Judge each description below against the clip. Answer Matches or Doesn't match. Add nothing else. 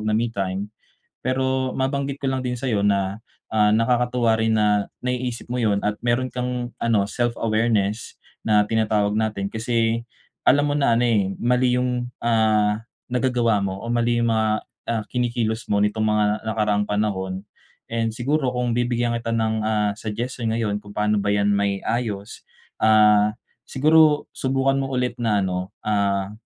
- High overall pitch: Doesn't match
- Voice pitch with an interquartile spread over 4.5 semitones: Doesn't match